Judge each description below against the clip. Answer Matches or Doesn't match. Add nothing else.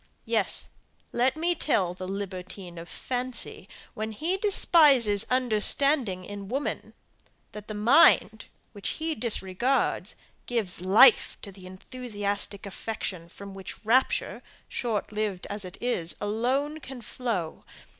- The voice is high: Matches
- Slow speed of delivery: Matches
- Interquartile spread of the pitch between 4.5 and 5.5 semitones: Matches